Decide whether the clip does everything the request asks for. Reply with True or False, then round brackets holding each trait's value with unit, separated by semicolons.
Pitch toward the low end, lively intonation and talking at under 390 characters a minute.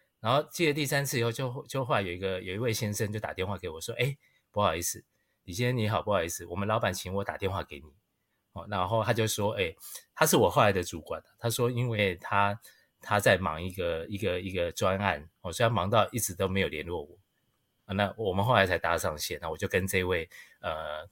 False (100 Hz; 4.0 semitones; 330 characters per minute)